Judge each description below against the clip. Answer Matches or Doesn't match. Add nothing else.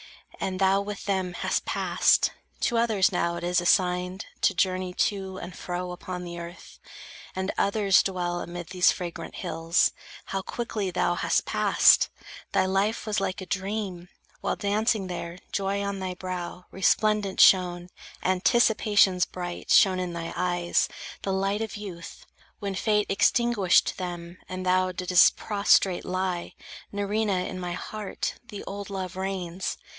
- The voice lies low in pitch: Doesn't match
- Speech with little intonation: Matches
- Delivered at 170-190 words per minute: Doesn't match